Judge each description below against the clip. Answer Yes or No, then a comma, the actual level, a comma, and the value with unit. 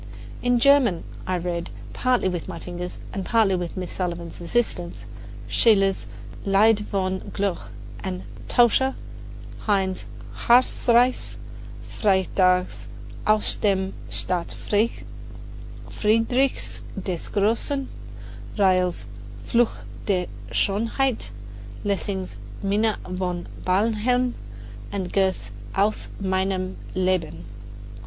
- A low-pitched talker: No, high, 195 Hz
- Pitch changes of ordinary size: Yes, average, 3.5 semitones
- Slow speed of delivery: Yes, slow, 90 wpm